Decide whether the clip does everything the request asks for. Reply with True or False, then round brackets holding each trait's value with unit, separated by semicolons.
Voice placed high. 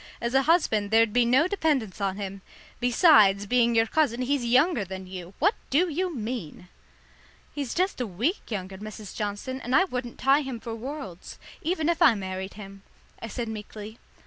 True (235 Hz)